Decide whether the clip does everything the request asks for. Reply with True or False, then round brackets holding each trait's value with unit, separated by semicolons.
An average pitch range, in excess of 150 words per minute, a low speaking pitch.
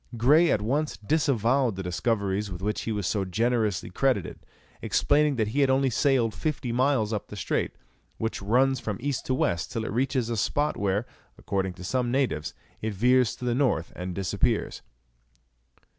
True (4.6 semitones; 175 wpm; 115 Hz)